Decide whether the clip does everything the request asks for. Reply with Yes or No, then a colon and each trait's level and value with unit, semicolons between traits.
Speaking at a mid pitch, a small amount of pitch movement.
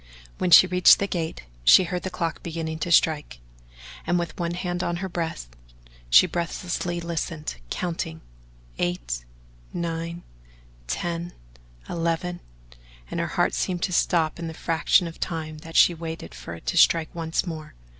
Yes: medium, 170 Hz; narrow, 1.7 semitones